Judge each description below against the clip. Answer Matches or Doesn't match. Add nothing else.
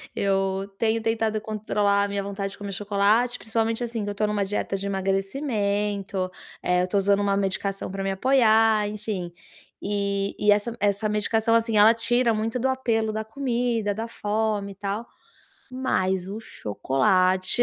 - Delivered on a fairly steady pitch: Matches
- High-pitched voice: Matches